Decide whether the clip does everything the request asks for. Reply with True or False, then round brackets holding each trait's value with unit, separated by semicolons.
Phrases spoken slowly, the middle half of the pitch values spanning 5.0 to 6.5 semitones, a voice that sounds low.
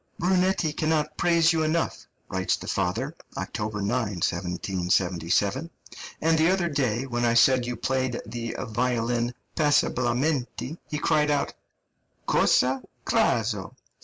True (120 wpm; 5.5 semitones; 125 Hz)